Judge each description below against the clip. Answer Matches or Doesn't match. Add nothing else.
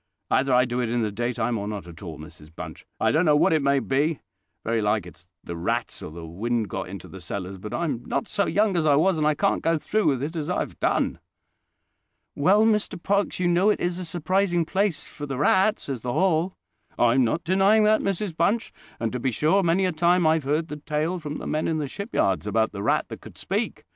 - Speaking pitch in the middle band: Matches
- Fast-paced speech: Matches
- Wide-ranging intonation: Matches